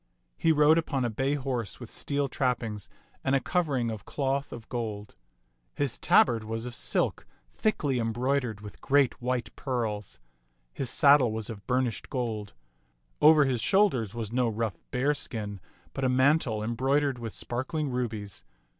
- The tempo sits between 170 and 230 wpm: No, average, 155 wpm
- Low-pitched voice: Yes, low, 125 Hz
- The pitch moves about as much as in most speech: Yes, average, 3.7 semitones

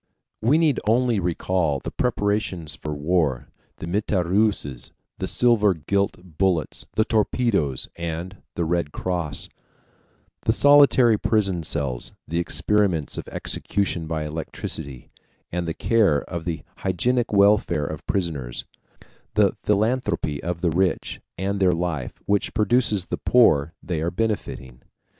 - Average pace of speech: No, slow, 130 wpm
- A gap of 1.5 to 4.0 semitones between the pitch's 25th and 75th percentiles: No, average, 4.9 semitones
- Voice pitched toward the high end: No, very low, 90 Hz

